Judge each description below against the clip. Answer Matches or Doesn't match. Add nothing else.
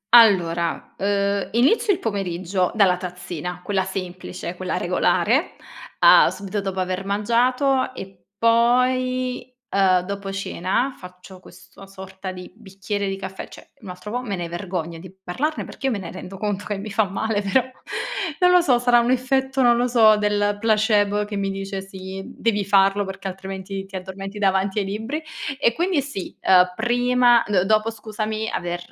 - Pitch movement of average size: Matches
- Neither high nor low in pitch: Doesn't match